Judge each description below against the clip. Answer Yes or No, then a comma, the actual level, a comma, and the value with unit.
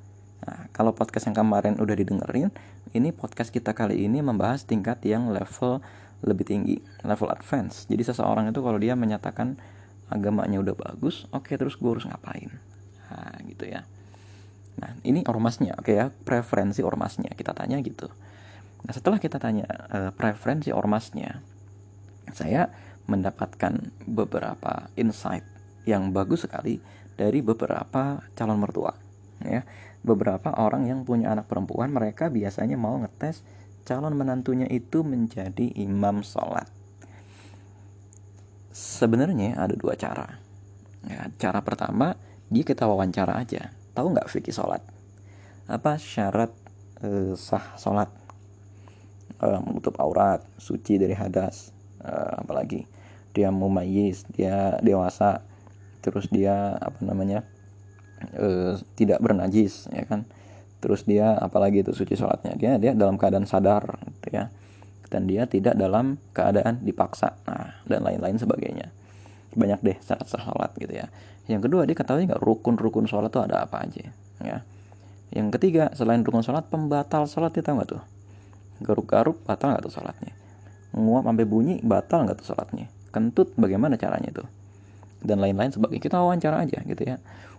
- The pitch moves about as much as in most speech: No, narrow, 2.3 semitones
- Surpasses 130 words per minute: Yes, fast, 140 wpm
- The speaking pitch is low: Yes, low, 100 Hz